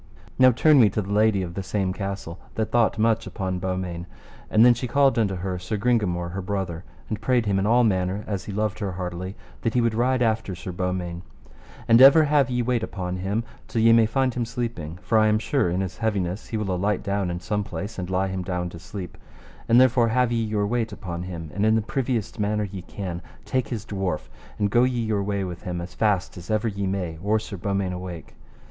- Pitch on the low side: Yes, low, 100 Hz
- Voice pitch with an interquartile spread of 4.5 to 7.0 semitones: No, average, 3.7 semitones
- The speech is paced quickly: Yes, fast, 230 wpm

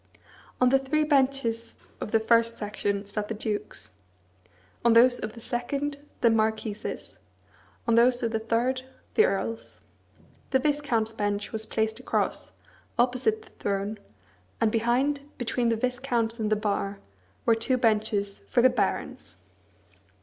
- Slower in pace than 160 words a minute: Yes, average, 140 wpm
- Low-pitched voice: No, high, 230 Hz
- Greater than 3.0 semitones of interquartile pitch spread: No, average, 2.7 semitones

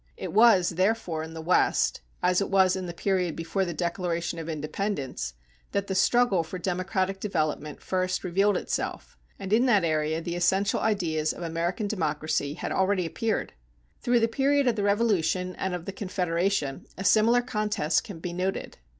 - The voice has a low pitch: No, medium, 185 Hz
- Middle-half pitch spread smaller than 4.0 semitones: Yes, average, 3.3 semitones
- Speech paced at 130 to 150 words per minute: No, average, 175 wpm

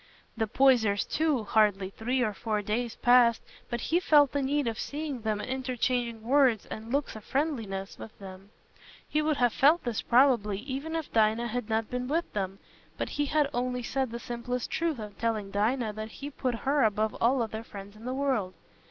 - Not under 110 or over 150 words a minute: No, average, 195 wpm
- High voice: Yes, high, 240 Hz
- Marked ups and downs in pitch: No, average, 3.8 semitones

